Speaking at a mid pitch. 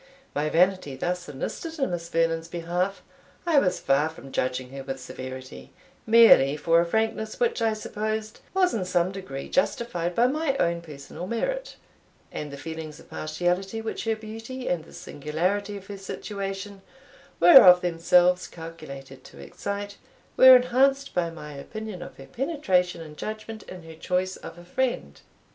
Yes: medium, 180 Hz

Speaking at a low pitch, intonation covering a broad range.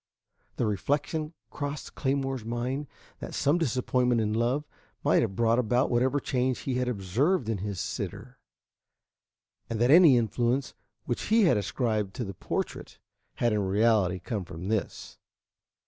No: low, 120 Hz; average, 4.0 semitones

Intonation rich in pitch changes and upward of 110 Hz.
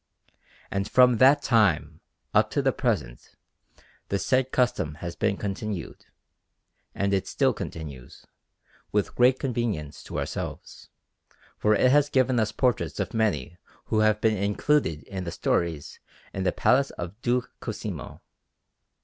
No: wide, 6.0 semitones; low, 105 Hz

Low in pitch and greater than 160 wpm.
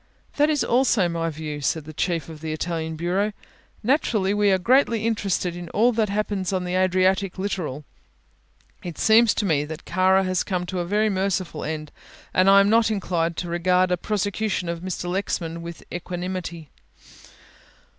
No: medium, 185 Hz; average, 175 wpm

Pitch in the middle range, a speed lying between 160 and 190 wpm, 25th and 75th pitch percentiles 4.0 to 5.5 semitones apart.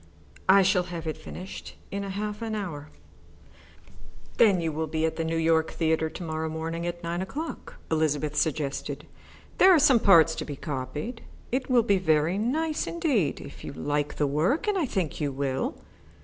Yes: medium, 165 Hz; average, 180 wpm; average, 5.2 semitones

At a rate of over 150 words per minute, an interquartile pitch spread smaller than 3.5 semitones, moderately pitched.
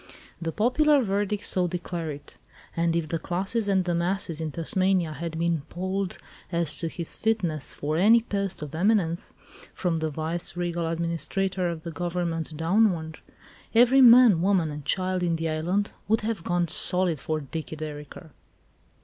Yes: average, 160 wpm; average, 3.1 semitones; medium, 175 Hz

